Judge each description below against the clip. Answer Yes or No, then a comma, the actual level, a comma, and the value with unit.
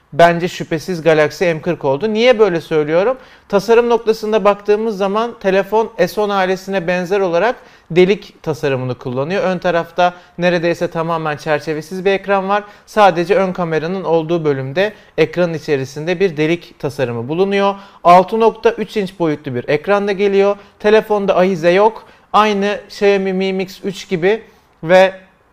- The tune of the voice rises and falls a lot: No, average, 3.4 semitones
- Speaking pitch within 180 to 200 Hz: Yes, high, 190 Hz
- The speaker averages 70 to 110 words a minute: No, average, 130 wpm